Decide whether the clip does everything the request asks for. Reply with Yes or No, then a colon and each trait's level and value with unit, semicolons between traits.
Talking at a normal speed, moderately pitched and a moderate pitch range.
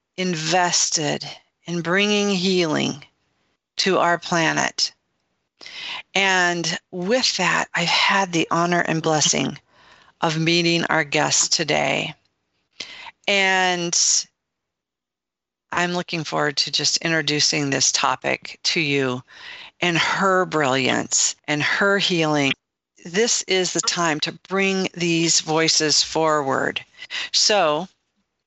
No: slow, 100 wpm; medium, 170 Hz; average, 3.6 semitones